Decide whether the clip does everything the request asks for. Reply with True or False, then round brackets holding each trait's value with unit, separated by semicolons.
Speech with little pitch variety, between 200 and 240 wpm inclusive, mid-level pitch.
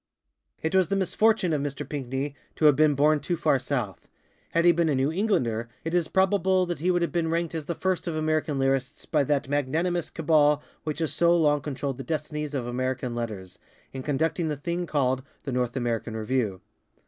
False (4.2 semitones; 205 wpm; 150 Hz)